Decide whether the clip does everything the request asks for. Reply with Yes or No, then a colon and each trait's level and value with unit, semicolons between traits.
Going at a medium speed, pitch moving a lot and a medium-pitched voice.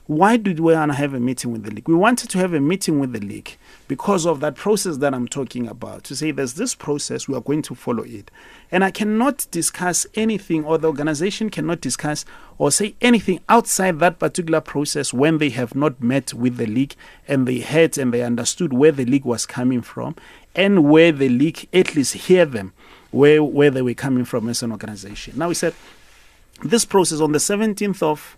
No: fast, 210 wpm; wide, 6.1 semitones; medium, 150 Hz